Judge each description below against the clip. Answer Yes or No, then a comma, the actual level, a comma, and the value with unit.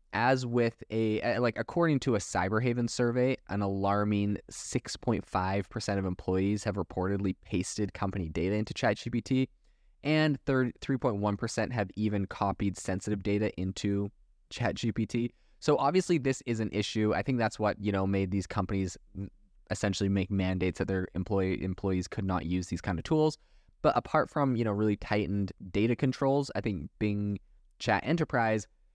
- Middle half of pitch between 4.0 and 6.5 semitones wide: No, average, 3.4 semitones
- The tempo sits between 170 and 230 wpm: No, average, 150 wpm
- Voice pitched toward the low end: Yes, low, 105 Hz